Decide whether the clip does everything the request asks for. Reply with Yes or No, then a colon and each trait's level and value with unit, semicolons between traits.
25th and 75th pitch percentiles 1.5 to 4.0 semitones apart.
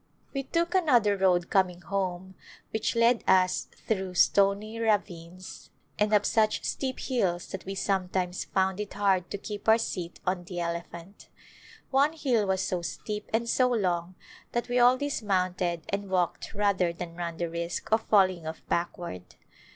Yes: average, 3.7 semitones